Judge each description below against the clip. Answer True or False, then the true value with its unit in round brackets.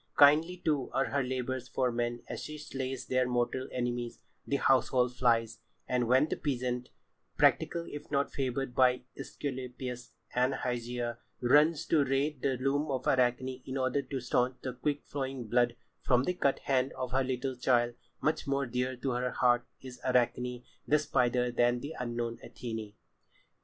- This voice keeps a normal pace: True (160 wpm)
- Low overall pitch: True (130 Hz)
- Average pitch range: False (1.8 semitones)